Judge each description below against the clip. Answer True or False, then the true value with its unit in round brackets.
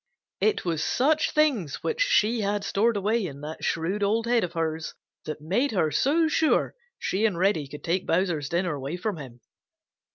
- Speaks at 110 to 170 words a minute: False (185 wpm)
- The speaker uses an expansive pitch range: True (6.2 semitones)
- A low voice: False (190 Hz)